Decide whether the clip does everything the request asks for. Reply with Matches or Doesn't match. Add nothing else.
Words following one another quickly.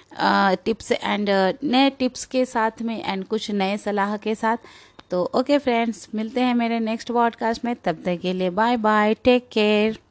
Doesn't match